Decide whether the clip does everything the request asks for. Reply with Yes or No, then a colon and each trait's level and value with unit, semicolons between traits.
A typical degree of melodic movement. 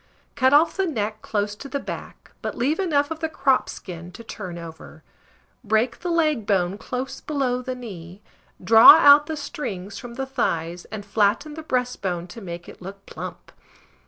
No: wide, 6.5 semitones